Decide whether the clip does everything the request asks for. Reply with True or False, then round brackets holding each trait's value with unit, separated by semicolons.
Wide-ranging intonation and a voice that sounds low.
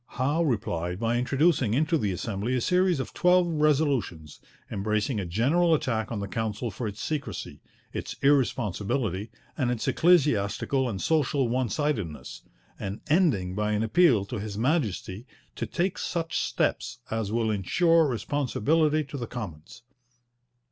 True (6.4 semitones; 120 Hz)